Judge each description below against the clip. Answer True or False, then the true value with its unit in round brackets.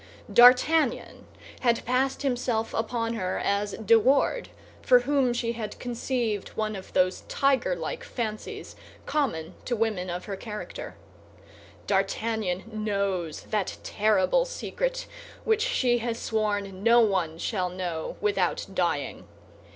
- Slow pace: True (120 wpm)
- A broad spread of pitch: False (4.1 semitones)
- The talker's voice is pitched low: False (225 Hz)